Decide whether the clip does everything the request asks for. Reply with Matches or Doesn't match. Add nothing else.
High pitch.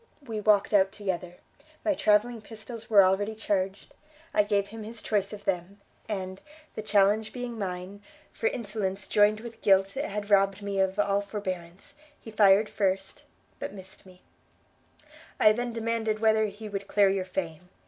Matches